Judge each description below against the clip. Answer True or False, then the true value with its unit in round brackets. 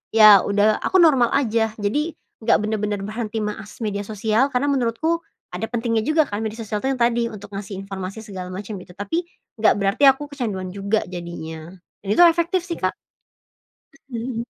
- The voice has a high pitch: True (220 Hz)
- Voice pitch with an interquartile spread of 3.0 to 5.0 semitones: True (3.6 semitones)